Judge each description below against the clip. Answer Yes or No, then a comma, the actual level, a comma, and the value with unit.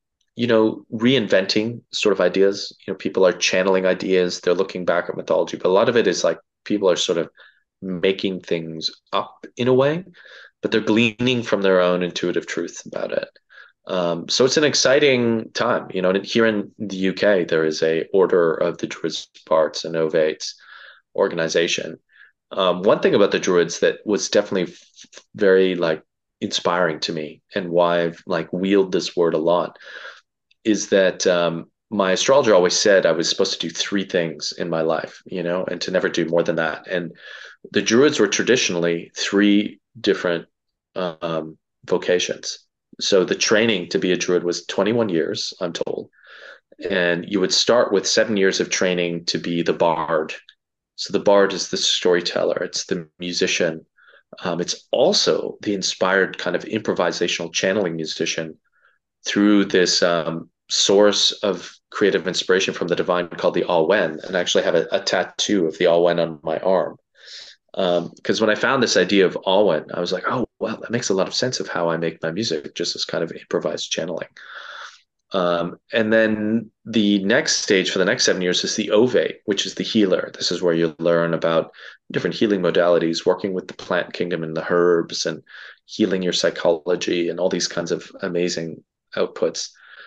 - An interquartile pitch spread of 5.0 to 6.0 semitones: No, average, 3.8 semitones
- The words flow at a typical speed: Yes, average, 185 wpm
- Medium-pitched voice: No, very low, 90 Hz